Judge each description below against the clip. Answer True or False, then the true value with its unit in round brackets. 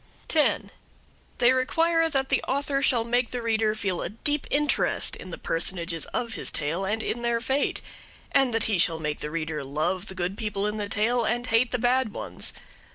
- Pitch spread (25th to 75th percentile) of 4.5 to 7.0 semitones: True (5.3 semitones)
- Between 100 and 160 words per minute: False (200 wpm)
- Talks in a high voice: True (225 Hz)